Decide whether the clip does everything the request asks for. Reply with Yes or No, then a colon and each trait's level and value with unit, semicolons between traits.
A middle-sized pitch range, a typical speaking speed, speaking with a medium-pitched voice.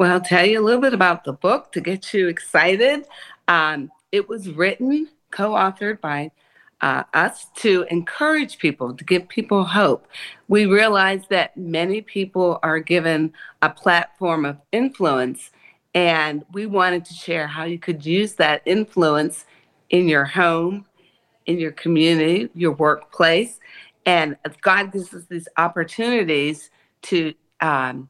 Yes: average, 3.9 semitones; average, 145 wpm; medium, 175 Hz